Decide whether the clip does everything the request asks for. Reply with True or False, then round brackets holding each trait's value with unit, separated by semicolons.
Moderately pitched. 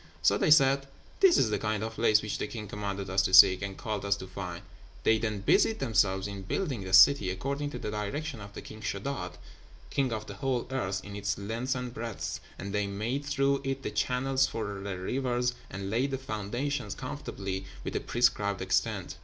False (110 Hz)